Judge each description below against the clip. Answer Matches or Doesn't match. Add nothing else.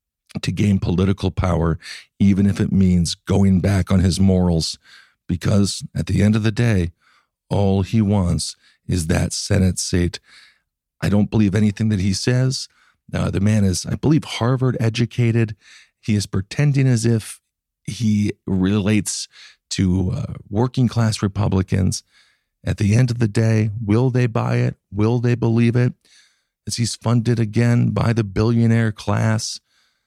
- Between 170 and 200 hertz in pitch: Doesn't match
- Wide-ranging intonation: Doesn't match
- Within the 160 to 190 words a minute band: Doesn't match